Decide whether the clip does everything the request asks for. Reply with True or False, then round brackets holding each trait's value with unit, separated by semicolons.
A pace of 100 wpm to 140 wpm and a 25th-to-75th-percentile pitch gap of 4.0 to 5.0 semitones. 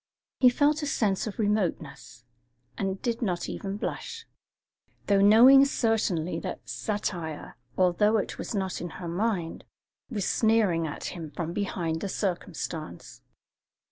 True (135 wpm; 4.6 semitones)